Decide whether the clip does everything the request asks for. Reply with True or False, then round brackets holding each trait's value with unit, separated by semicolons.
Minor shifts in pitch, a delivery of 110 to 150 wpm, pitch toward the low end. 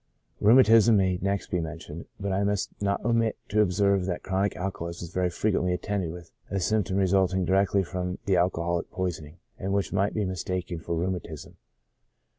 False (2.2 semitones; 175 wpm; 95 Hz)